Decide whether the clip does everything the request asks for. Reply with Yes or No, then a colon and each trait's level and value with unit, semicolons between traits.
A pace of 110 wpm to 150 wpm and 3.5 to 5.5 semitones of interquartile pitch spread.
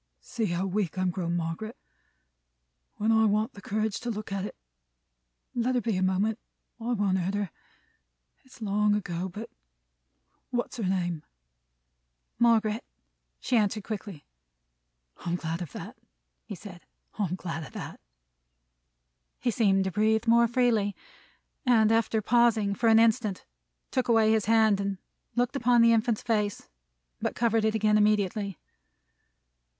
No: average, 145 wpm; average, 2.9 semitones